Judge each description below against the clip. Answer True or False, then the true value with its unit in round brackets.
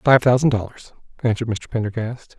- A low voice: True (115 Hz)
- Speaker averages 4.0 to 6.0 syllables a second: True (5.9 syllables/s)